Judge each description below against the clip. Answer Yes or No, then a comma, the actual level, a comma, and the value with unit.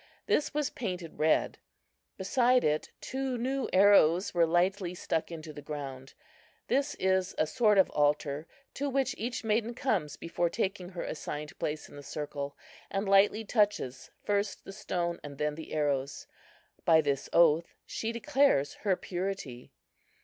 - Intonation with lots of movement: Yes, wide, 6.0 semitones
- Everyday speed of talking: Yes, average, 150 wpm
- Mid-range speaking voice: Yes, medium, 180 Hz